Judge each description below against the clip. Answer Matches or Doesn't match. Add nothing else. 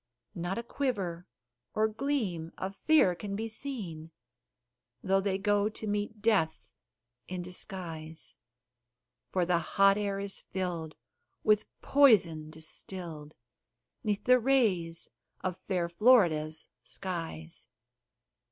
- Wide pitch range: Doesn't match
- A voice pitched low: Doesn't match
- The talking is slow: Matches